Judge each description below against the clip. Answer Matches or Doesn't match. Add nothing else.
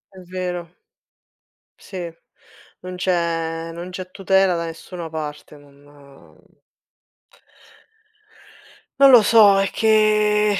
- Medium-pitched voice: Matches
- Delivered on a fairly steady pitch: Doesn't match